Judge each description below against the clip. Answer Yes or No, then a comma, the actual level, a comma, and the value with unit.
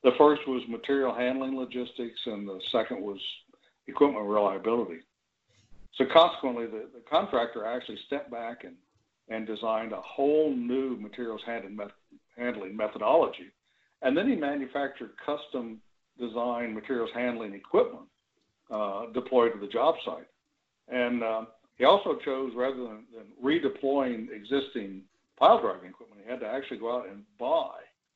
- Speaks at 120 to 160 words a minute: Yes, average, 145 wpm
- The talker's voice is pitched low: Yes, low, 120 Hz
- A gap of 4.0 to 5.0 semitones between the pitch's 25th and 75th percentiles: No, average, 3.4 semitones